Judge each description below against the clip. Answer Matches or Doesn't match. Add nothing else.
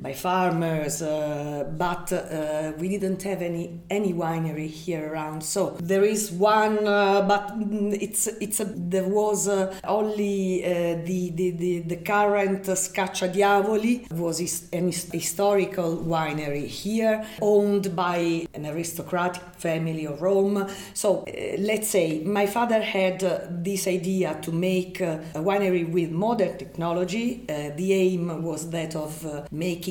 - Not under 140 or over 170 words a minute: Matches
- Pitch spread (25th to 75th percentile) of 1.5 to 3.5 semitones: Matches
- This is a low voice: Doesn't match